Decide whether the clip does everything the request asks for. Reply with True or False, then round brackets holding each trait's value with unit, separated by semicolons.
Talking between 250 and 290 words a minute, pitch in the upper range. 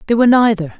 False (225 wpm; 220 Hz)